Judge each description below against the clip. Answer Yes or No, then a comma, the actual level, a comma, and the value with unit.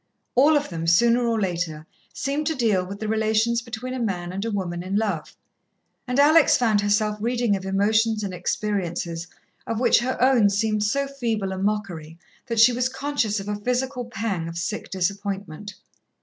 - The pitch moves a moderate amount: Yes, average, 3.8 semitones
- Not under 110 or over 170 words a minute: No, average, 180 wpm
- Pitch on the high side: Yes, high, 215 Hz